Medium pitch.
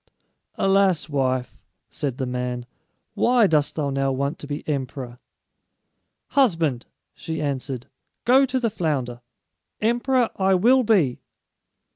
Yes: medium, 150 Hz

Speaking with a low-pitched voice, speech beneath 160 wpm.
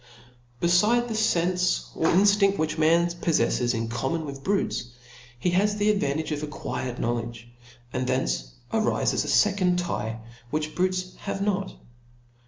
No: medium, 170 Hz; average, 140 wpm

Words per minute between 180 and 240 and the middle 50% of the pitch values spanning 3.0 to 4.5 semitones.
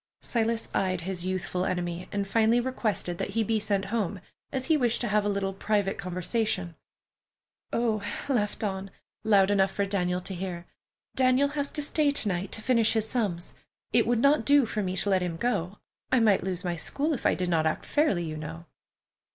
Yes: average, 200 wpm; average, 4.2 semitones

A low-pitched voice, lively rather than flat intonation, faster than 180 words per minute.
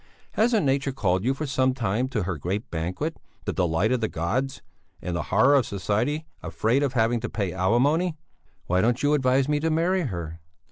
Yes: low, 120 Hz; wide, 7.1 semitones; average, 195 wpm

